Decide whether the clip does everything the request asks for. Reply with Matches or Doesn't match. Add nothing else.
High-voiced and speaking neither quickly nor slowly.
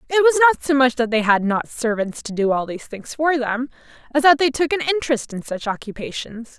Doesn't match